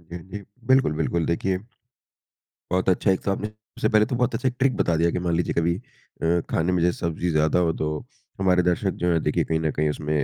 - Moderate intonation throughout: Yes, average, 3.5 semitones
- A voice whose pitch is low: Yes, very low, 90 Hz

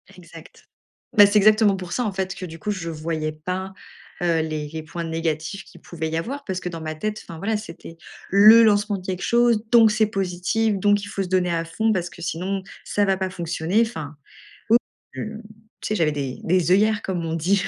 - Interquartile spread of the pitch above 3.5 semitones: Yes, average, 4.1 semitones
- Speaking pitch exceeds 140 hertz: Yes, medium, 185 Hz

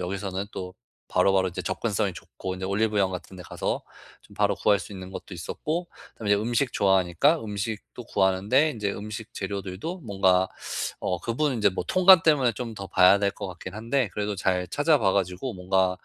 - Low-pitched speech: Yes, low, 100 Hz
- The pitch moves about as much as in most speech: Yes, average, 3.7 semitones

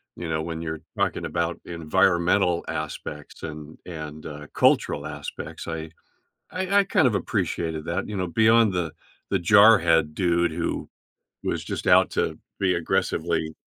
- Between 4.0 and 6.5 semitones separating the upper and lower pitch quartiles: No, average, 2.9 semitones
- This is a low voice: Yes, very low, 85 Hz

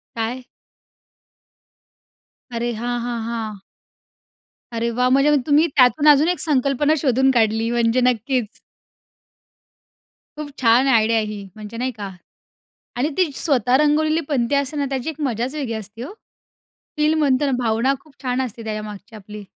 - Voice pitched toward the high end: Yes, very high, 250 Hz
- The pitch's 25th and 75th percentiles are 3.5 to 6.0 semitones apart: Yes, average, 3.9 semitones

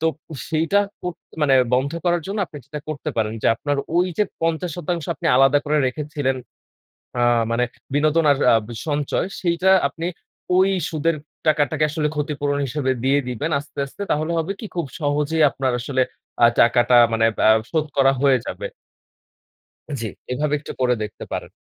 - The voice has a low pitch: No, medium, 150 Hz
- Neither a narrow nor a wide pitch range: Yes, average, 3.1 semitones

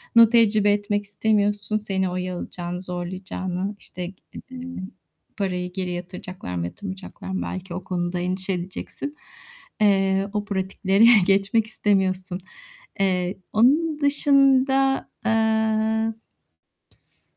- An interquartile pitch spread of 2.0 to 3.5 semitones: Yes, average, 3.2 semitones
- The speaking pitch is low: No, high, 195 Hz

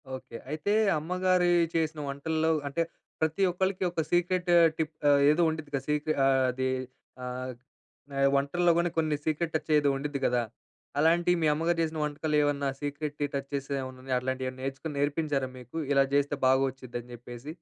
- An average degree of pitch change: Yes, average, 3.0 semitones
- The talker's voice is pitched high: No, medium, 145 Hz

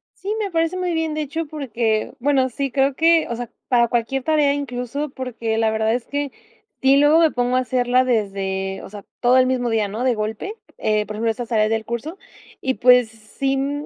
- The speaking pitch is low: No, very high, 250 Hz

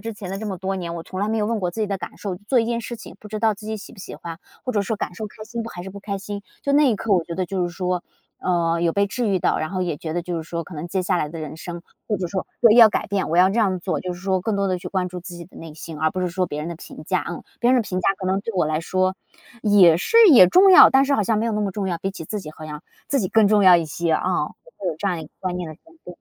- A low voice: No, high, 190 Hz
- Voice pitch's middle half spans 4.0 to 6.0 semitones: No, average, 3.5 semitones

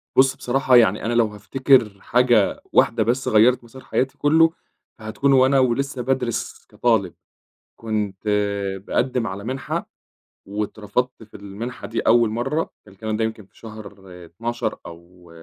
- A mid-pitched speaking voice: No, low, 115 Hz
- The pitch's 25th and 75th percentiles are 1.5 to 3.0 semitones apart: No, average, 3.4 semitones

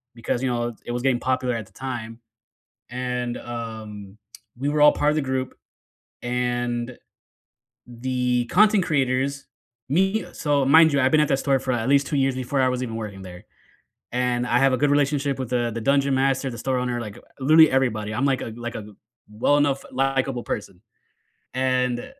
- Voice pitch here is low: Yes, low, 130 Hz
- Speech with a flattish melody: Yes, narrow, 2.3 semitones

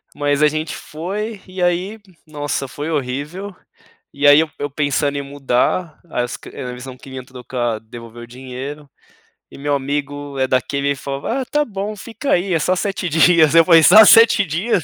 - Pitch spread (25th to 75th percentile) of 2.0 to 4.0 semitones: No, average, 4.8 semitones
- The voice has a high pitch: No, medium, 145 Hz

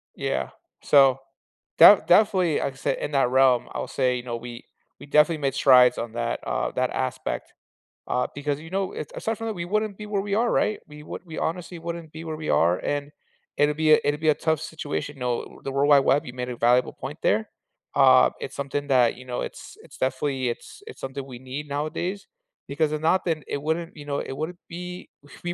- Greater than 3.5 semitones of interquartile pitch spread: Yes, average, 4.2 semitones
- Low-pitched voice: No, medium, 145 Hz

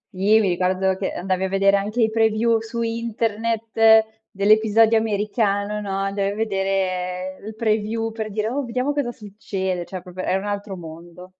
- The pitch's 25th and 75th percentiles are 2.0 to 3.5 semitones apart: Yes, average, 2.7 semitones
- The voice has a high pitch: Yes, high, 210 Hz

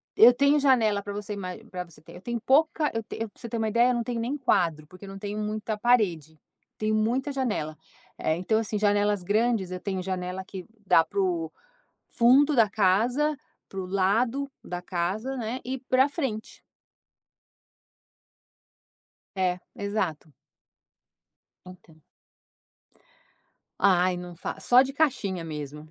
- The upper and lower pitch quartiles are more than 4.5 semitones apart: Yes, average, 5.1 semitones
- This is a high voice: Yes, high, 210 Hz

